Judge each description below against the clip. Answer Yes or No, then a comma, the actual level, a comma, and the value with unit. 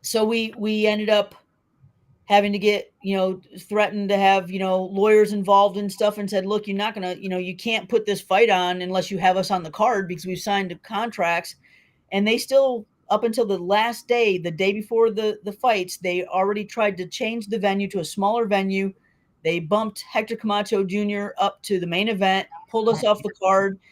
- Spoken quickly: Yes, fast, 215 wpm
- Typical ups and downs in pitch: No, narrow, 2.3 semitones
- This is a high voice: Yes, high, 200 Hz